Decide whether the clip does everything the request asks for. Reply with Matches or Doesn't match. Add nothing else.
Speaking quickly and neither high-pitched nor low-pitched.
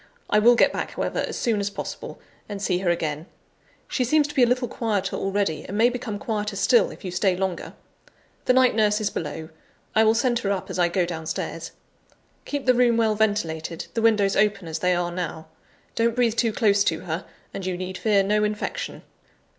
Doesn't match